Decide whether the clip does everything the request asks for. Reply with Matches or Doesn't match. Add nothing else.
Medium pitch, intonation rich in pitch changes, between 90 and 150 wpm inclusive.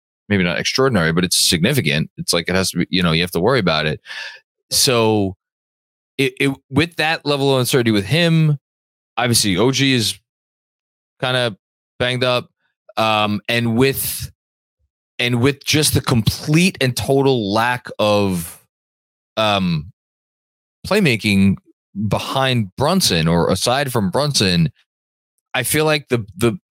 Doesn't match